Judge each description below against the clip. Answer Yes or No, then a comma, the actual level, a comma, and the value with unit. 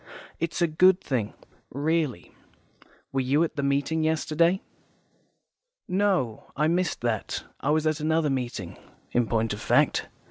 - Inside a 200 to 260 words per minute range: No, average, 140 wpm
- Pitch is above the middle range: No, medium, 150 Hz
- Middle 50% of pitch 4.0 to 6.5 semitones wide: Yes, average, 4.5 semitones